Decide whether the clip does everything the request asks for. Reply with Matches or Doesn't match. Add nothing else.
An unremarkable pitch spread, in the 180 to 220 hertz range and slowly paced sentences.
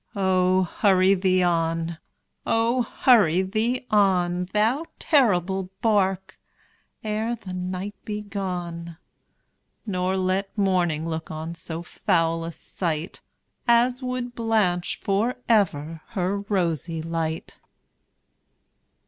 Matches